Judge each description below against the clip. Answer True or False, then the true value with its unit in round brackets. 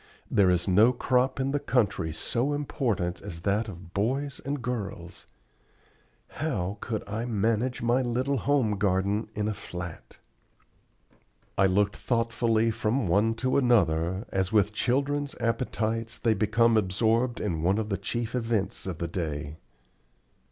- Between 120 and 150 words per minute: True (145 wpm)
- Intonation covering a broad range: False (4.2 semitones)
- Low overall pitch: True (110 Hz)